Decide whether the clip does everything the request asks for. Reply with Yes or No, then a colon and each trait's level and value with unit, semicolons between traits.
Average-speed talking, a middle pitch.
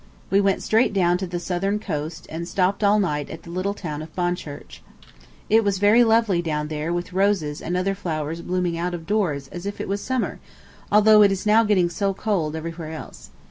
No: fast, 210 wpm; medium, 180 Hz